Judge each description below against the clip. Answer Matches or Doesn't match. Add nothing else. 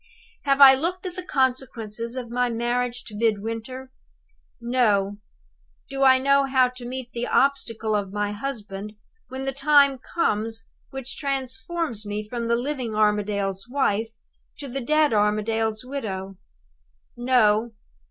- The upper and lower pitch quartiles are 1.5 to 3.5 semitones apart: Doesn't match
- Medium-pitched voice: Doesn't match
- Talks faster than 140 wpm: Doesn't match